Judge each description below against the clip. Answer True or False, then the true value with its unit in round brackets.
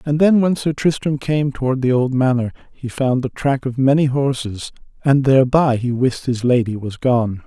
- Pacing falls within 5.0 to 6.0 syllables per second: False (4.8 syllables/s)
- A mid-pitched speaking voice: False (130 Hz)